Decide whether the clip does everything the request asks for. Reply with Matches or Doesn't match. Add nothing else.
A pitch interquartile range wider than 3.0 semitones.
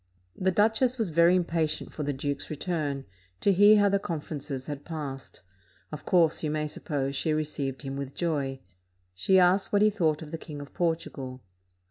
Matches